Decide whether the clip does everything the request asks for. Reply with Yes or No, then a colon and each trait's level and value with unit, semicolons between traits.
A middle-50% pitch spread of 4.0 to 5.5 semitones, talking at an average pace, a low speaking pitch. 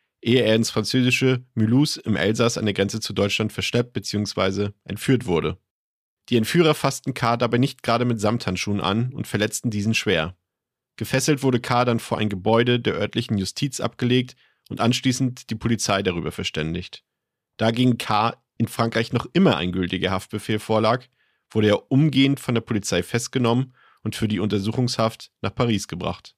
No: average, 3.2 semitones; average, 165 wpm; low, 115 Hz